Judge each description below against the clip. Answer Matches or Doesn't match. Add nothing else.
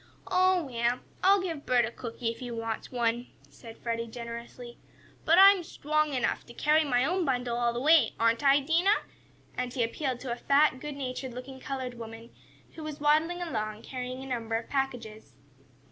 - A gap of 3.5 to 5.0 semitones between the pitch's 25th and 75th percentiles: Matches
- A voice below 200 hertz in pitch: Doesn't match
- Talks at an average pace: Matches